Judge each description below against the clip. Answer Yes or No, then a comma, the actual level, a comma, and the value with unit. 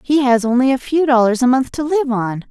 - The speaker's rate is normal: No, fast, 265 wpm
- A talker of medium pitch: No, very high, 255 Hz